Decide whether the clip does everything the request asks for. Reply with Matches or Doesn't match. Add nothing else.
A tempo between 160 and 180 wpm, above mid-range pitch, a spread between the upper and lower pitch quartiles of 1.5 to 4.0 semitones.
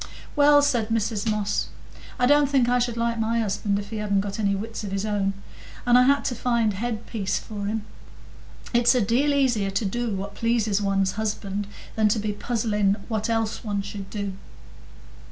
Doesn't match